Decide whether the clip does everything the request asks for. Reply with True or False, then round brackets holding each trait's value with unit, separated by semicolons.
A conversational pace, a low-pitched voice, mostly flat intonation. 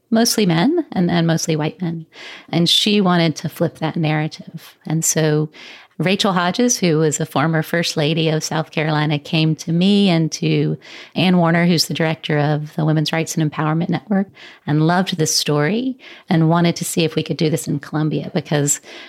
False (190 wpm; 160 Hz; 2.3 semitones)